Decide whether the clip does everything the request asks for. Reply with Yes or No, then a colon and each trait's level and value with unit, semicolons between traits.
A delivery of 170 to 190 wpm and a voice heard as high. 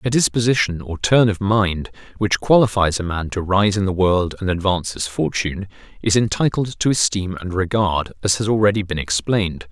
No: average, 185 wpm; low, 100 Hz